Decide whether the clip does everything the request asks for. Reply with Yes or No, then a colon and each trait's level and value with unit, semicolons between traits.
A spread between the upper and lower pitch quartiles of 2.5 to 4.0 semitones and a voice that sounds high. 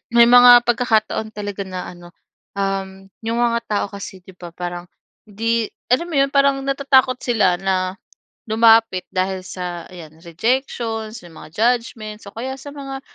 No: average, 4.6 semitones; high, 215 Hz